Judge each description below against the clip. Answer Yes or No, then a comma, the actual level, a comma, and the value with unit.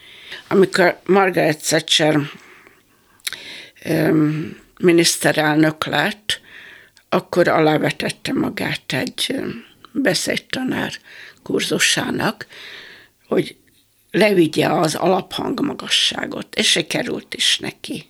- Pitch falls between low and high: Yes, medium, 160 Hz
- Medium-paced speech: No, slow, 70 wpm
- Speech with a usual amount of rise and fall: Yes, average, 3.6 semitones